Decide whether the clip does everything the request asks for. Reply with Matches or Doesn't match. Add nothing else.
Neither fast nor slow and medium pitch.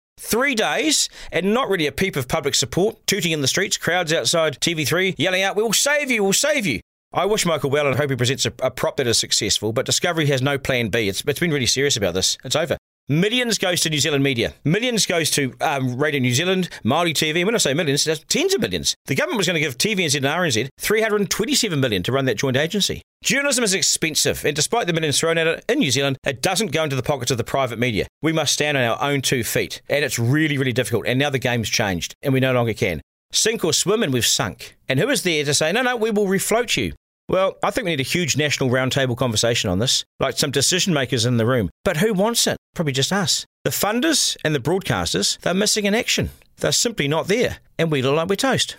Doesn't match